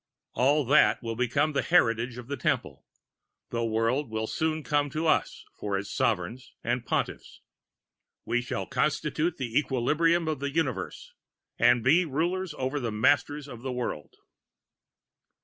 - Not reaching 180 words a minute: Yes, average, 150 wpm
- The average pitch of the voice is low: Yes, low, 130 Hz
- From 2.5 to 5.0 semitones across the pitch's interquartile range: Yes, average, 4.4 semitones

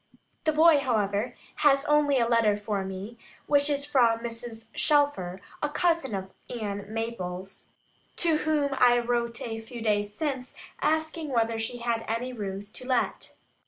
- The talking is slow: No, average, 155 wpm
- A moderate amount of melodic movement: Yes, average, 4.9 semitones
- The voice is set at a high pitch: Yes, high, 235 Hz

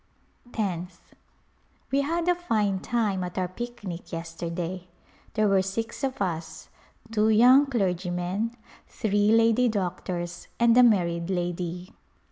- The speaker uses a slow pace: Yes, slow, 120 wpm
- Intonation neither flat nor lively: Yes, average, 4.5 semitones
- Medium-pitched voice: No, high, 195 Hz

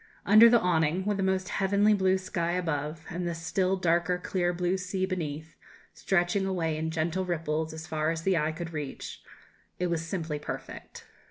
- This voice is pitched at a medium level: Yes, medium, 175 Hz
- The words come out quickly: No, average, 180 wpm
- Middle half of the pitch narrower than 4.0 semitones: Yes, average, 2.8 semitones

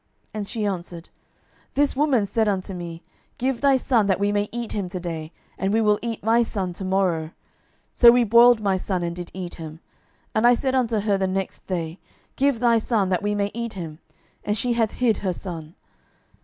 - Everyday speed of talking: No, fast, 215 wpm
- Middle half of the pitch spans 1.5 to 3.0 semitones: No, average, 4.3 semitones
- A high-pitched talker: Yes, high, 205 Hz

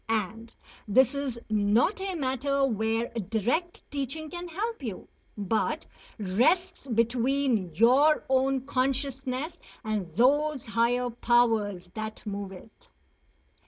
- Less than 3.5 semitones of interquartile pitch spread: No, average, 4.3 semitones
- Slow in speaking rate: Yes, slow, 110 wpm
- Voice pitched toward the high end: Yes, high, 245 Hz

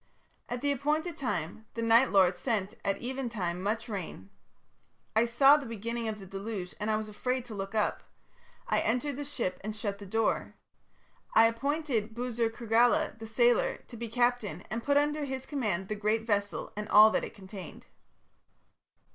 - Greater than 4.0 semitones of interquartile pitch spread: No, average, 3.3 semitones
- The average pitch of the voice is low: No, high, 225 Hz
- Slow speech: No, average, 180 wpm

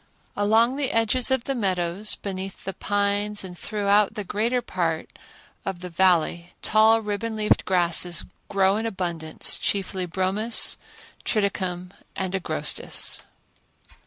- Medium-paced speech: No, slow, 125 wpm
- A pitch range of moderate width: Yes, average, 3.1 semitones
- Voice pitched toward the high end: Yes, high, 195 Hz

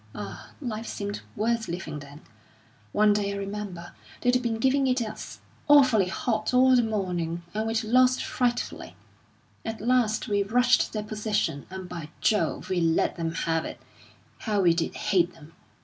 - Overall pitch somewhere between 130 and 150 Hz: No, high, 210 Hz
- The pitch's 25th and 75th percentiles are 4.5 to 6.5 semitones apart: Yes, average, 4.8 semitones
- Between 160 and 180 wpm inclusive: Yes, average, 165 wpm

